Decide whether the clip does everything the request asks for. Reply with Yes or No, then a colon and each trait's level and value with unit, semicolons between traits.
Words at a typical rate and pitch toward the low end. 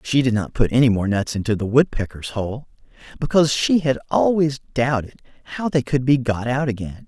Yes: average, 195 wpm; low, 125 Hz